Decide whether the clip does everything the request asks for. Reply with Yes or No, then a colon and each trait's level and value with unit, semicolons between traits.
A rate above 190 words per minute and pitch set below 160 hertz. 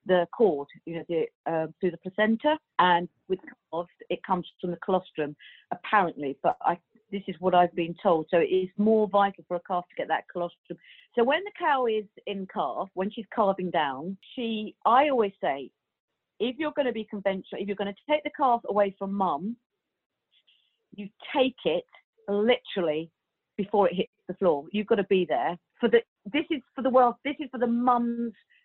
No: average, 200 wpm; high, 205 Hz